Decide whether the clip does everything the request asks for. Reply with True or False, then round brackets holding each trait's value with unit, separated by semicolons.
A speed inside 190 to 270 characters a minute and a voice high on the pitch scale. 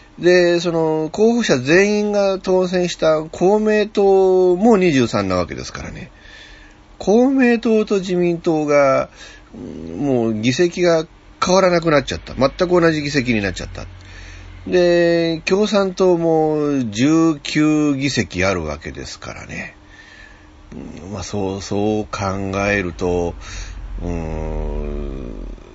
False (205 characters per minute; 150 Hz)